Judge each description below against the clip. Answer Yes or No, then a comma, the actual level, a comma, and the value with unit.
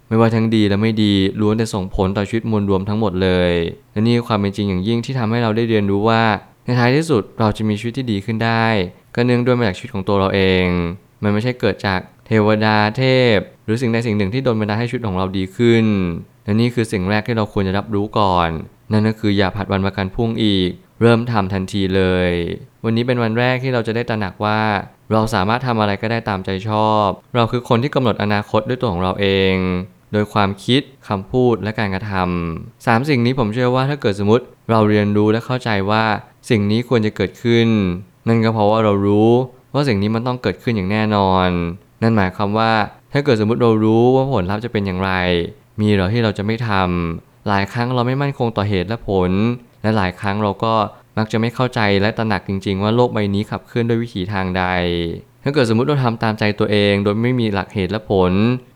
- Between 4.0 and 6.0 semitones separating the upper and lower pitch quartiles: No, average, 3.1 semitones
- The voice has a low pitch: Yes, low, 110 Hz